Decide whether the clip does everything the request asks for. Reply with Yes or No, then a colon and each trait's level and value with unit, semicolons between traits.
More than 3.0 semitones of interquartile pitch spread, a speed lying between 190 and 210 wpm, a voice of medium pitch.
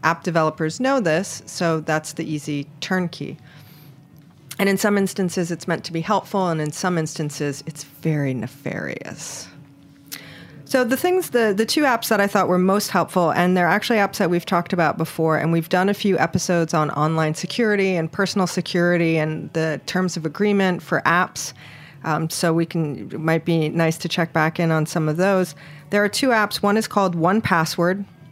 Yes: average, 3.6 semitones; average, 195 wpm; medium, 170 Hz